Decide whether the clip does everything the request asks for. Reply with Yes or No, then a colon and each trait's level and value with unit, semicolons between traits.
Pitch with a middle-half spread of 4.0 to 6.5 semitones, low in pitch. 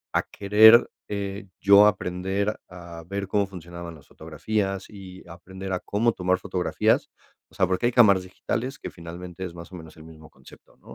No: narrow, 2.6 semitones; very low, 95 Hz